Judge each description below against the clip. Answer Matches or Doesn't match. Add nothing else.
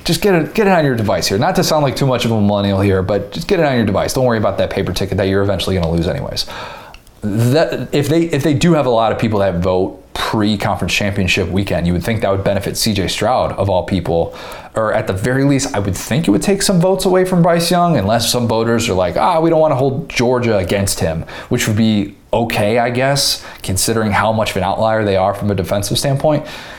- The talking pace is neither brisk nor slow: Doesn't match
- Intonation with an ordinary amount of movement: Doesn't match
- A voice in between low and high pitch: Doesn't match